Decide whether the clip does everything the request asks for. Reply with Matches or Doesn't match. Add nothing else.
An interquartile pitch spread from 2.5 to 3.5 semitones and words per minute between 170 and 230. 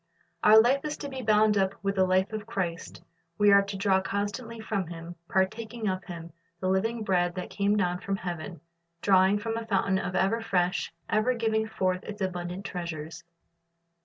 Matches